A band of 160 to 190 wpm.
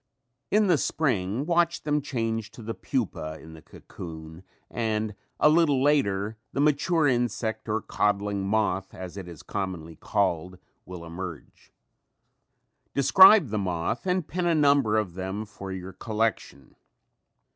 No: average, 140 wpm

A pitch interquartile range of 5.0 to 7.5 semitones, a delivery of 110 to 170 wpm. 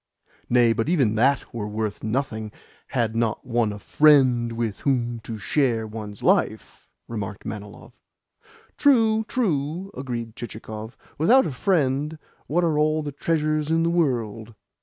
Yes: wide, 5.5 semitones; average, 140 wpm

